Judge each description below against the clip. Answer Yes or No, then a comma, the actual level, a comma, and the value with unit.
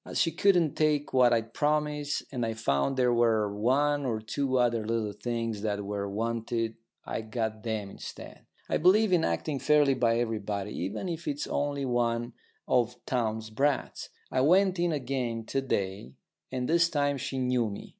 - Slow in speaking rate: No, average, 175 wpm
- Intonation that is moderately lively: Yes, average, 4.5 semitones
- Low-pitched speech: Yes, low, 120 Hz